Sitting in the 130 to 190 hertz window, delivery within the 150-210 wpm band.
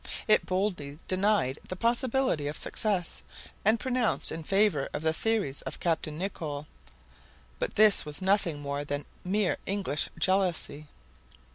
No: medium, 185 Hz; slow, 135 wpm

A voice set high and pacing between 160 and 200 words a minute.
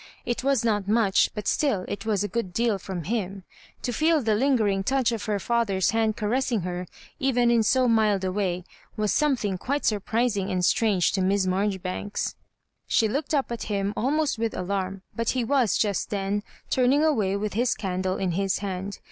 Yes: high, 210 Hz; average, 195 wpm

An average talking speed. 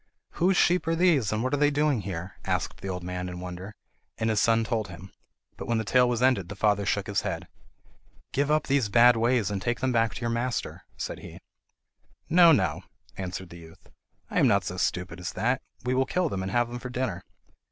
No: fast, 225 wpm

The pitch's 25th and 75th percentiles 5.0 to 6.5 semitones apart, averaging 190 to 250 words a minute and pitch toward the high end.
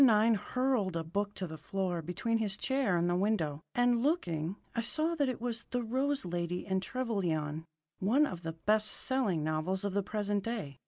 Yes: wide, 5.5 semitones; average, 195 wpm; high, 200 Hz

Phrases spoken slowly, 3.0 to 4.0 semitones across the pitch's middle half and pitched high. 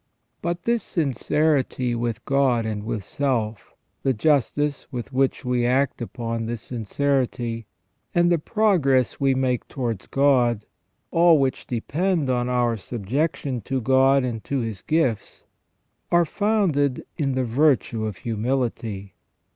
No: slow, 130 wpm; average, 3.6 semitones; low, 130 Hz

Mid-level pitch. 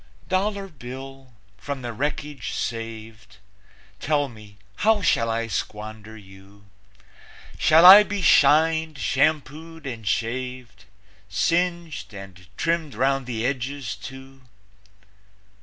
No: low, 130 Hz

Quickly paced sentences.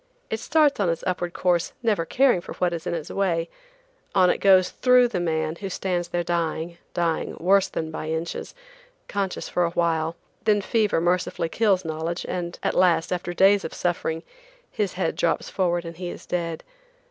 No: average, 185 wpm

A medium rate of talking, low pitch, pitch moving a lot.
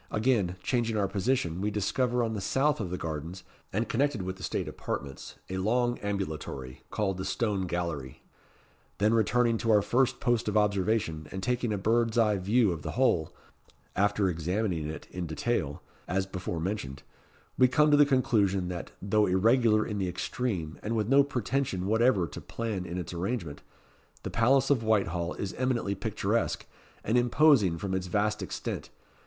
No: average, 170 wpm; low, 105 Hz; average, 4.5 semitones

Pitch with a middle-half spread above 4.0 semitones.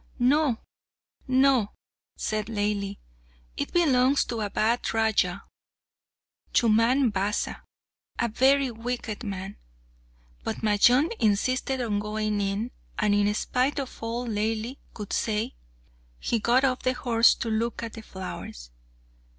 No: average, 3.2 semitones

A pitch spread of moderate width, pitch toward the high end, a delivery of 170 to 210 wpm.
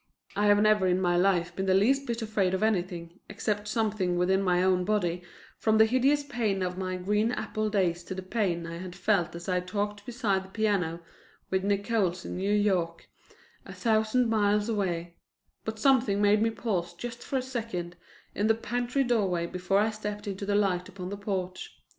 Yes: average, 3.1 semitones; high, 200 Hz; average, 195 wpm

